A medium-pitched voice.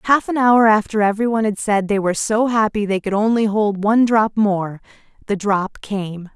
No: high, 210 Hz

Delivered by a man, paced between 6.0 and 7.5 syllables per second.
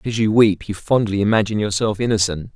Yes: male; 6.8 syllables/s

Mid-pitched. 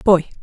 Yes: medium, 180 Hz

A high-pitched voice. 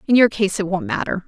Yes: high, 200 Hz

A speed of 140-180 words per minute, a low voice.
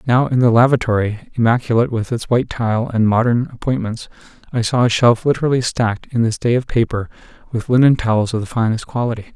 No: average, 190 wpm; low, 120 Hz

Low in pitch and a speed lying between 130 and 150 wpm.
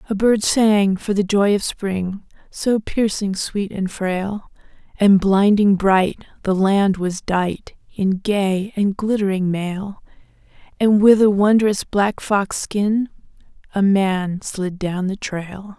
No: high, 200 Hz; average, 145 wpm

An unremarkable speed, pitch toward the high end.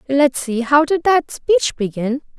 Yes: average, 150 wpm; very high, 280 Hz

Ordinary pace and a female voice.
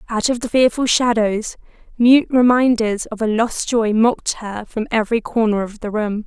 Yes: average, 180 wpm; female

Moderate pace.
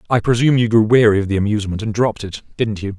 No: fast, 260 wpm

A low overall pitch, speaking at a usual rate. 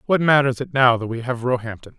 No: low, 130 Hz; fast, 240 wpm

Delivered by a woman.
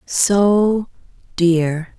Yes: female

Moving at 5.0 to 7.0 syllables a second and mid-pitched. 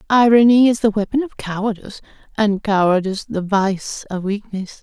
No: 5.2 syllables/s; high, 210 Hz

